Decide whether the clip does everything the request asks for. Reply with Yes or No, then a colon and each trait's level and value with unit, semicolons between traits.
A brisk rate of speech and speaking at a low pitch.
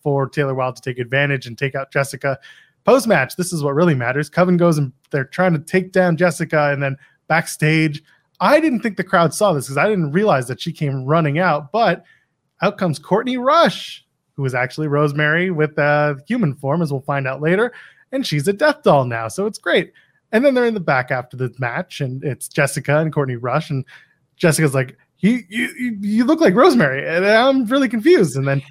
No: fast, 215 wpm; medium, 155 Hz